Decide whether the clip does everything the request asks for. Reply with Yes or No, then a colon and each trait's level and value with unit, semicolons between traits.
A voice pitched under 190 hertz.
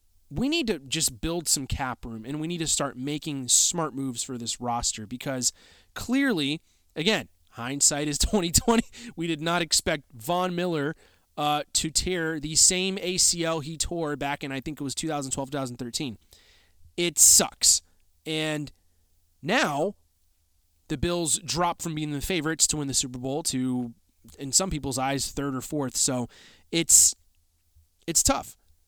Yes: medium, 140 Hz